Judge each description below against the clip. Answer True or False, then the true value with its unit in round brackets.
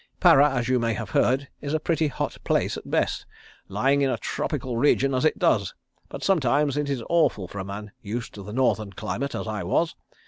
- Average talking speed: False (215 wpm)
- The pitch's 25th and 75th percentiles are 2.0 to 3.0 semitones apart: False (4.9 semitones)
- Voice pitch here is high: False (130 Hz)